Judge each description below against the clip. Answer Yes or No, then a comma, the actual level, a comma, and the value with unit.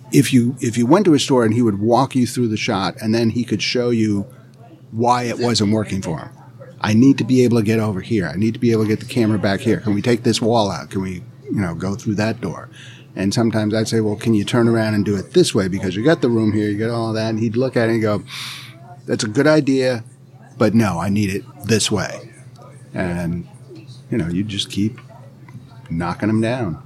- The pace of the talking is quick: Yes, fast, 255 wpm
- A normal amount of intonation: Yes, average, 3.1 semitones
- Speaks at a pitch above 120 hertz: No, low, 115 Hz